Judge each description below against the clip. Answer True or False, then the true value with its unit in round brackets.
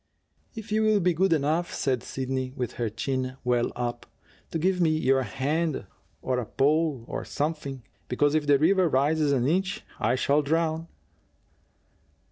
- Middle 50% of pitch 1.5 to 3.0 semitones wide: False (4.1 semitones)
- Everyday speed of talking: True (160 wpm)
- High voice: False (145 Hz)